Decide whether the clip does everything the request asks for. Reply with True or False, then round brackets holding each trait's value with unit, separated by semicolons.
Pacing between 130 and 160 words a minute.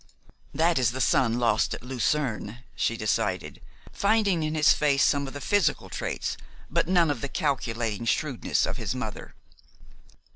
True (155 wpm)